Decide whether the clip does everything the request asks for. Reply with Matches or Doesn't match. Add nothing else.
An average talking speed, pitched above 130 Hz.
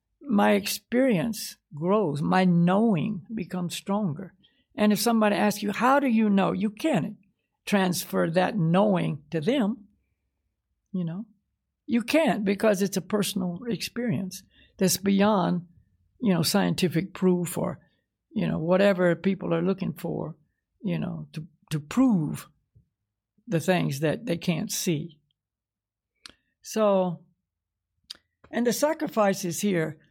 Doesn't match